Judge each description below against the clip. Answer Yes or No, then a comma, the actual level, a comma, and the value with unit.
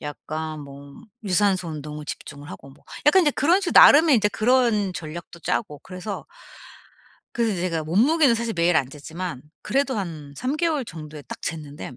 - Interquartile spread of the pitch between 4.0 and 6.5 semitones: No, wide, 7.6 semitones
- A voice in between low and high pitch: Yes, medium, 175 Hz